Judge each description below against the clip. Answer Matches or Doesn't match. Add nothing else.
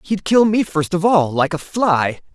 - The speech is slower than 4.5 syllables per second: Matches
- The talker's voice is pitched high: Doesn't match